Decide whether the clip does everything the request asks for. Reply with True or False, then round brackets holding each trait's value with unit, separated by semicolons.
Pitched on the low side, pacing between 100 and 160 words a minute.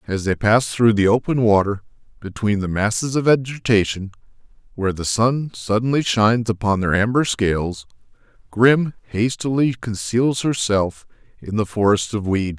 True (110 Hz; 145 wpm)